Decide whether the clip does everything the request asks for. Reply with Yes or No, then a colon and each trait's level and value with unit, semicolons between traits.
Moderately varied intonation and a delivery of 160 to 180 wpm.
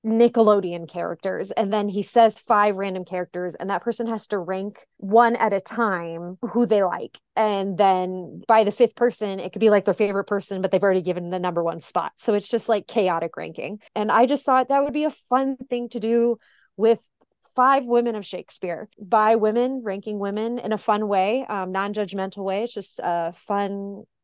No: average, 3.4 semitones; fast, 205 wpm